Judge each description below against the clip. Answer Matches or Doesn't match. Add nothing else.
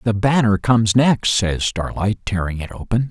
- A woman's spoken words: Doesn't match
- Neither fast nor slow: Matches